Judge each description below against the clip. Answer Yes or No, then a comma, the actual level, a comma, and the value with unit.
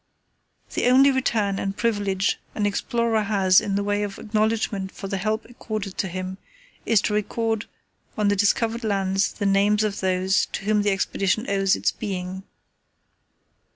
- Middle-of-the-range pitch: No, high, 205 Hz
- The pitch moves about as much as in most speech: No, narrow, 1.9 semitones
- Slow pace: No, average, 155 wpm